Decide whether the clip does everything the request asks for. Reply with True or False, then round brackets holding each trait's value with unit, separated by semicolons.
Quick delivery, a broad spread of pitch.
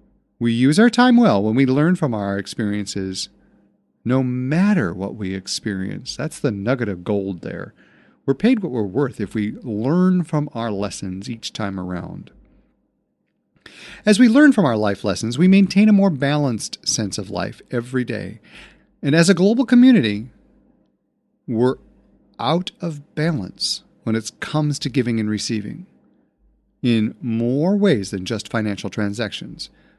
False (150 wpm; 8.0 semitones)